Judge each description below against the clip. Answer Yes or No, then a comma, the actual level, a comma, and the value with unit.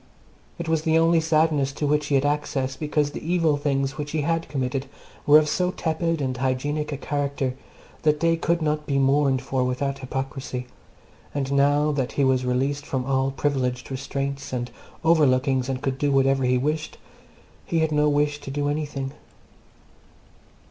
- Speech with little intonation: Yes, narrow, 2.2 semitones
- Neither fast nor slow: Yes, average, 175 wpm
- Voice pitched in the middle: Yes, medium, 145 Hz